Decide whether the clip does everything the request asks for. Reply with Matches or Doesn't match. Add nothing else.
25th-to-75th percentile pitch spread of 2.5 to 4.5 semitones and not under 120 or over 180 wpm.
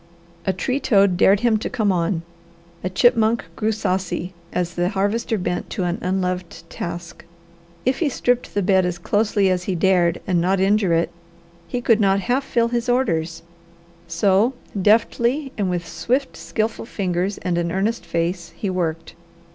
Matches